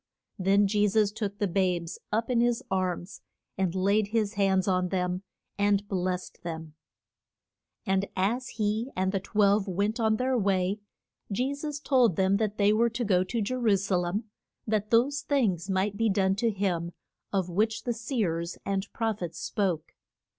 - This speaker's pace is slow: No, average, 175 wpm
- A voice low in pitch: No, high, 200 Hz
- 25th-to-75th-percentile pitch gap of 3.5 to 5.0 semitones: No, average, 3.0 semitones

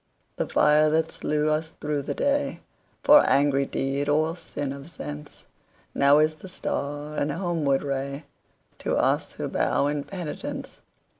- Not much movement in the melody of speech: Yes, narrow, 2.0 semitones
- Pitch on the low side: No, medium, 150 Hz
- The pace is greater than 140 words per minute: No, slow, 135 wpm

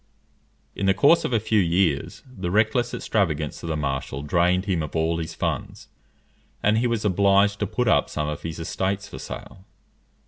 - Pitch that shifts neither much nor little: Yes, average, 4.3 semitones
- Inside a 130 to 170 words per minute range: No, average, 185 wpm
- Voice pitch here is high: No, very low, 95 Hz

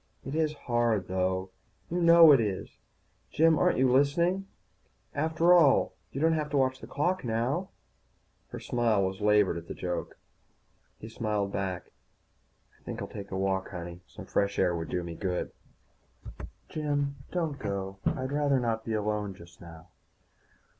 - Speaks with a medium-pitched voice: No, low, 115 Hz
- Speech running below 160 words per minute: No, average, 165 wpm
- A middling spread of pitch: No, wide, 7.4 semitones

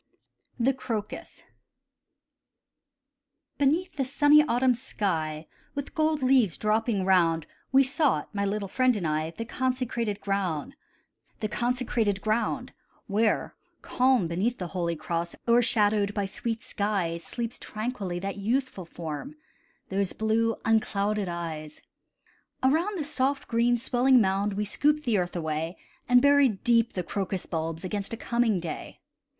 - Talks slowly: Yes, slow, 125 wpm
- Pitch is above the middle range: Yes, high, 215 Hz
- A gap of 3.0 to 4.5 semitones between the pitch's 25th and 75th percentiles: No, average, 5.2 semitones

